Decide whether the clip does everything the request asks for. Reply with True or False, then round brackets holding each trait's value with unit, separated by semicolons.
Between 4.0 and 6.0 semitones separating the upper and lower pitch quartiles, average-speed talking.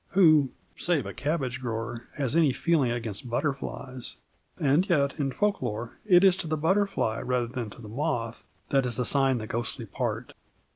True (4.8 semitones; 175 wpm)